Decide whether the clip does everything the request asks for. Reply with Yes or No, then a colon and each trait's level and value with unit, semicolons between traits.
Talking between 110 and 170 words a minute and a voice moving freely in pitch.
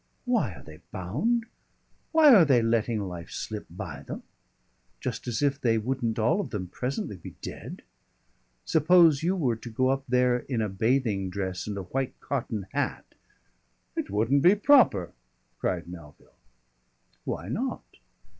Yes: average, 155 wpm; wide, 6.7 semitones